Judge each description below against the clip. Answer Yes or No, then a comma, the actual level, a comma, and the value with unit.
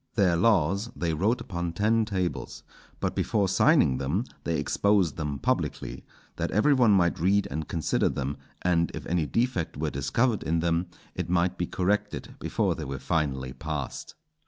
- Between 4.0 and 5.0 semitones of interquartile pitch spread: Yes, average, 4.7 semitones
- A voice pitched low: Yes, very low, 85 Hz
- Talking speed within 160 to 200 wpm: Yes, average, 165 wpm